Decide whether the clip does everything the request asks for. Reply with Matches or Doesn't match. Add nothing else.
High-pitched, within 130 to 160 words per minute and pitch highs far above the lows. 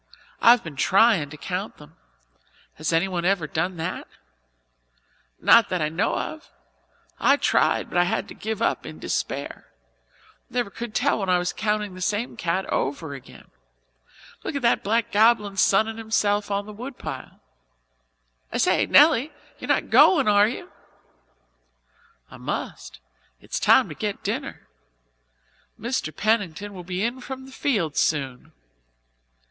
Doesn't match